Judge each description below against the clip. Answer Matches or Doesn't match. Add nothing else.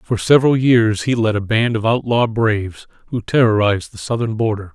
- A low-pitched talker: Matches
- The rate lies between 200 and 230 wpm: Doesn't match